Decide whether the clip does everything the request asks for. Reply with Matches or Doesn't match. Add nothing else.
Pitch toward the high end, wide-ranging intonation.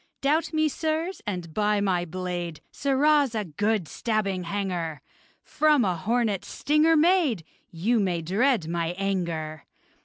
Matches